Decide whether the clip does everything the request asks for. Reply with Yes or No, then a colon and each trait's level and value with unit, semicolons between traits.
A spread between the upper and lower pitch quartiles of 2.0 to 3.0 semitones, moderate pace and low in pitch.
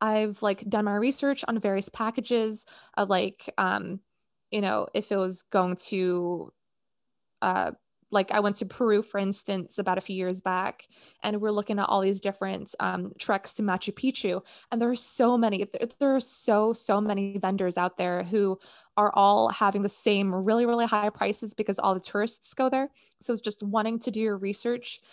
No: narrow, 2.6 semitones; average, 190 wpm; high, 205 Hz